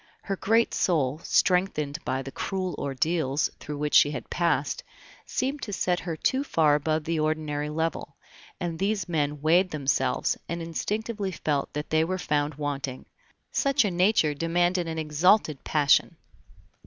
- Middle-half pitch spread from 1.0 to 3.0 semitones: No, average, 3.7 semitones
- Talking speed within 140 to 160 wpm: Yes, average, 155 wpm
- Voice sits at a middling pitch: Yes, medium, 160 Hz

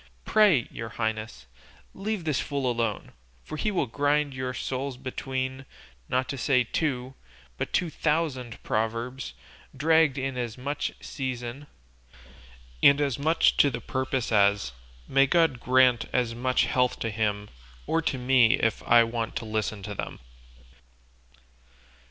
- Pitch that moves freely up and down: No, average, 3.4 semitones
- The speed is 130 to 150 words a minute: Yes, average, 145 wpm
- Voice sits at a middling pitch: No, low, 130 Hz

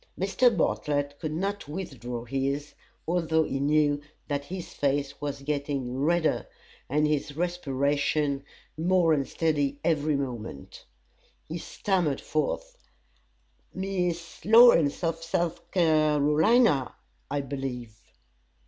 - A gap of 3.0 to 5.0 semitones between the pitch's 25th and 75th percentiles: Yes, average, 3.4 semitones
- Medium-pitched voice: Yes, medium, 150 Hz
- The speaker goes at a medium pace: No, slow, 105 wpm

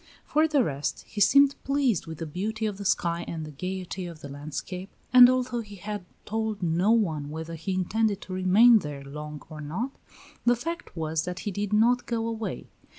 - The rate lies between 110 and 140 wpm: No, average, 200 wpm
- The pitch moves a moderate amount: No, wide, 5.7 semitones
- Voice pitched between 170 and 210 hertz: Yes, high, 190 Hz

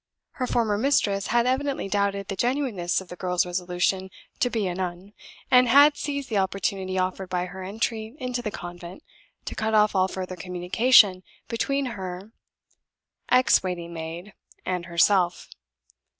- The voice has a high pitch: Yes, high, 195 Hz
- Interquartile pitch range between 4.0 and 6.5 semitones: Yes, average, 4.5 semitones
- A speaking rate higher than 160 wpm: No, average, 150 wpm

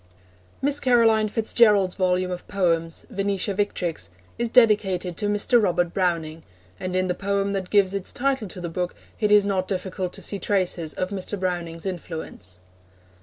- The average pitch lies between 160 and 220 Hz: Yes, high, 190 Hz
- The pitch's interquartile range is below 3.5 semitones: Yes, narrow, 2.6 semitones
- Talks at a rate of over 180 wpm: No, average, 170 wpm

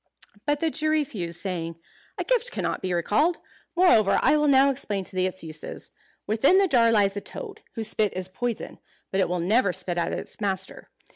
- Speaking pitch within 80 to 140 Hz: No, high, 210 Hz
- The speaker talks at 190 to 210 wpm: Yes, average, 200 wpm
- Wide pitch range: Yes, wide, 7.2 semitones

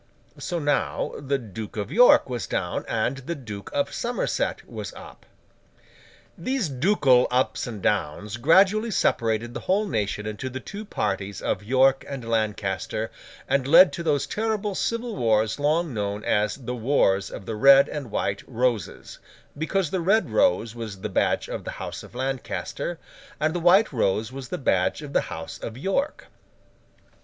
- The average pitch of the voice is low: Yes, low, 130 Hz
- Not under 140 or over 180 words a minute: Yes, average, 165 wpm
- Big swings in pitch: Yes, wide, 7.9 semitones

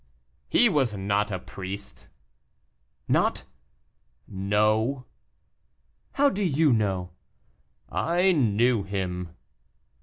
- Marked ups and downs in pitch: Yes, wide, 6.3 semitones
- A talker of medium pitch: No, low, 105 Hz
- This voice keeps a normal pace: No, slow, 85 wpm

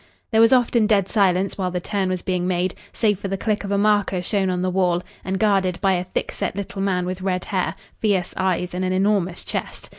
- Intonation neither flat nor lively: No, narrow, 1.8 semitones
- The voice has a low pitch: No, high, 190 Hz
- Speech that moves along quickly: Yes, fast, 235 wpm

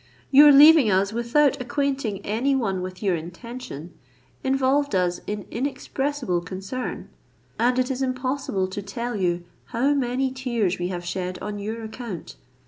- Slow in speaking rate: No, average, 145 wpm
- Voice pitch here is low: No, high, 235 Hz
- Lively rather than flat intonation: Yes, wide, 5.8 semitones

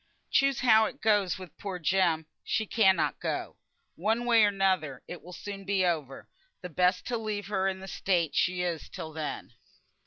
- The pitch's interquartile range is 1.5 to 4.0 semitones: Yes, average, 2.9 semitones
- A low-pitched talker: No, high, 190 Hz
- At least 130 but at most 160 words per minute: No, average, 185 wpm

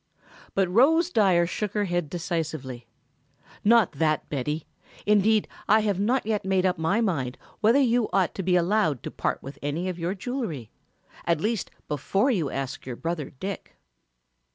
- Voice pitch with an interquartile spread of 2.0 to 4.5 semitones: No, wide, 5.5 semitones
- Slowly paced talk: No, average, 165 wpm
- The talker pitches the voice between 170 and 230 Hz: Yes, medium, 185 Hz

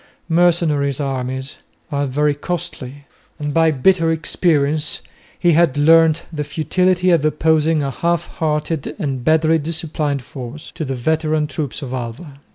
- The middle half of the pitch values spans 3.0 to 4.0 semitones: No, narrow, 2.6 semitones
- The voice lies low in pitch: No, medium, 150 Hz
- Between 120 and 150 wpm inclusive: Yes, average, 140 wpm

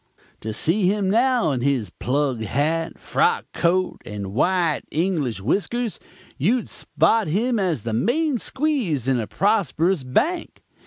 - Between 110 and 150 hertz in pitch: No, medium, 175 Hz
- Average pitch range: No, wide, 9.0 semitones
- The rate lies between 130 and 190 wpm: Yes, average, 140 wpm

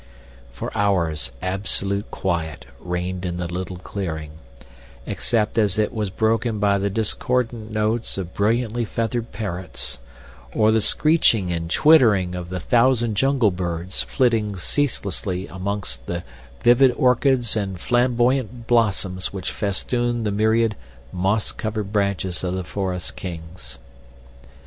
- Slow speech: Yes, slow, 125 wpm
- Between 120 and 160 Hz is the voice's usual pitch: No, low, 100 Hz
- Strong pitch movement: No, average, 4.1 semitones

